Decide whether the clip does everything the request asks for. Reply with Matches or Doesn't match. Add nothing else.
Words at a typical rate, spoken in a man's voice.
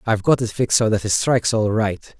Doesn't match